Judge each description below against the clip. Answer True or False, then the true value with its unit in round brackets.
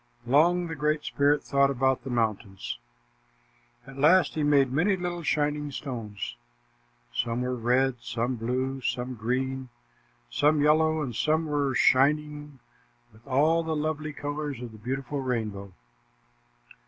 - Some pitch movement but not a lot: True (3.5 semitones)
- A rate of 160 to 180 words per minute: False (135 wpm)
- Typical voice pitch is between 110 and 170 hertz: True (135 Hz)